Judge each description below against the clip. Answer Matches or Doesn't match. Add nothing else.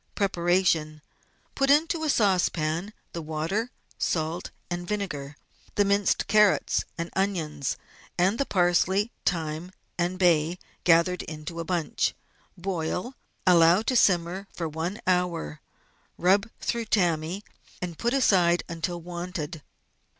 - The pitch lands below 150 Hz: Doesn't match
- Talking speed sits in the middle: Doesn't match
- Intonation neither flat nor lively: Matches